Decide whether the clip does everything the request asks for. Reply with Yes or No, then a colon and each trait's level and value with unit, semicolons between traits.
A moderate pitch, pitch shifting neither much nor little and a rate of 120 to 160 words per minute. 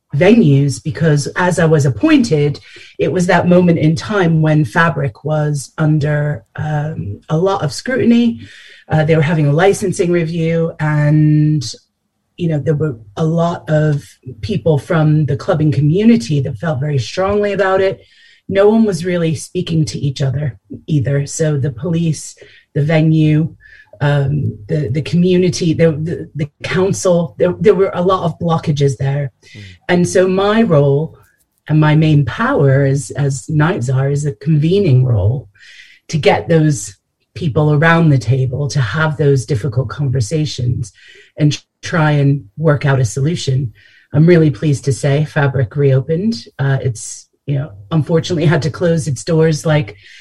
Yes: medium, 155 Hz; average, 3.1 semitones; average, 155 wpm